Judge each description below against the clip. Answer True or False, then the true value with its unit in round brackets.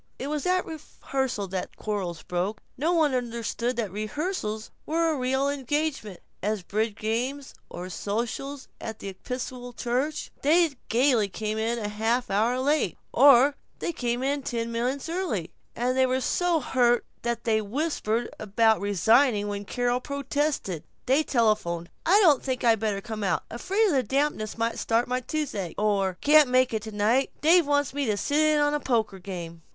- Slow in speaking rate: False (175 wpm)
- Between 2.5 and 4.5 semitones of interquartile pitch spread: False (4.9 semitones)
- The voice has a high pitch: True (245 Hz)